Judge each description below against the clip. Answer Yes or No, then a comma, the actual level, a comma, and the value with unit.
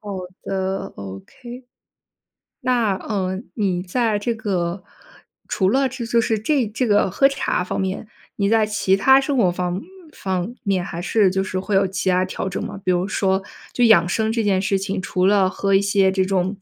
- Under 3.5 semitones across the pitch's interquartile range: Yes, average, 2.9 semitones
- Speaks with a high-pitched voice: Yes, high, 195 Hz